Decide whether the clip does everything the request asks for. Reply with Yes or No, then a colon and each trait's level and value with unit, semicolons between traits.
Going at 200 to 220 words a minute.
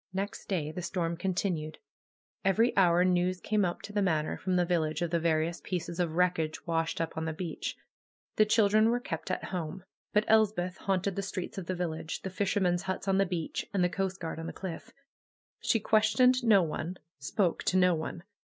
Yes: fast, 205 wpm